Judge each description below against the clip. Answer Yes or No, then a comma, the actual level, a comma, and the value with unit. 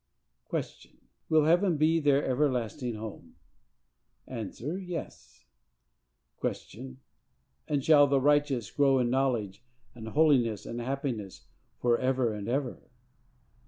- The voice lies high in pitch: No, low, 130 Hz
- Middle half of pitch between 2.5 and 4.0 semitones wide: No, average, 4.5 semitones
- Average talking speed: No, slow, 105 wpm